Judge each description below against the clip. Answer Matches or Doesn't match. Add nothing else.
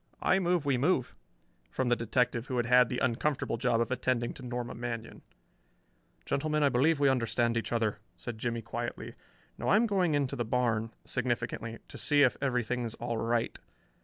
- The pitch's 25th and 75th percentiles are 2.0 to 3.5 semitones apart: Matches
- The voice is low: Matches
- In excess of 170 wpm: Matches